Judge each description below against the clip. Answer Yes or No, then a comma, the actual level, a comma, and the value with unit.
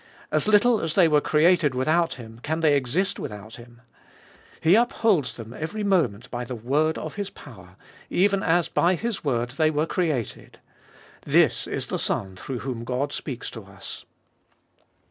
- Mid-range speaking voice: Yes, medium, 150 Hz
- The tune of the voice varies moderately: No, wide, 6.5 semitones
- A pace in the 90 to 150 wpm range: No, average, 165 wpm